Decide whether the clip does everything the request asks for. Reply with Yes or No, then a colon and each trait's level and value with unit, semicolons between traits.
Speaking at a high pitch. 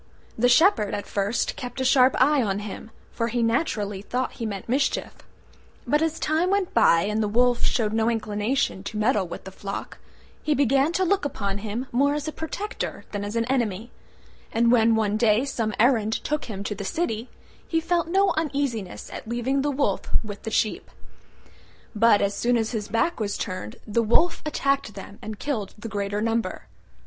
Yes: high, 230 Hz